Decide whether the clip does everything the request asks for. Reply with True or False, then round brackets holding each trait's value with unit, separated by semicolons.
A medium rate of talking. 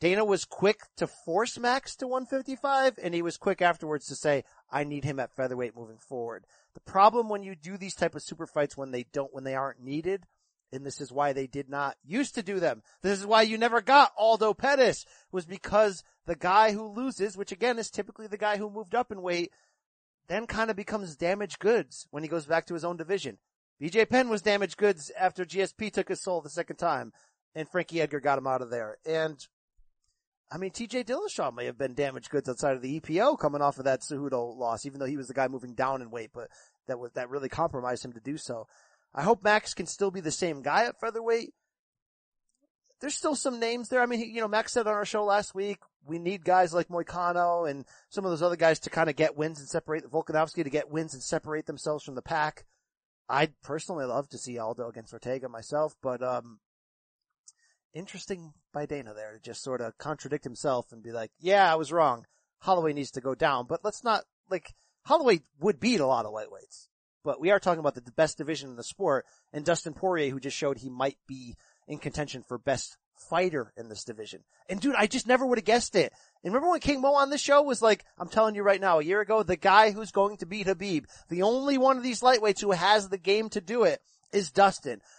False (230 wpm)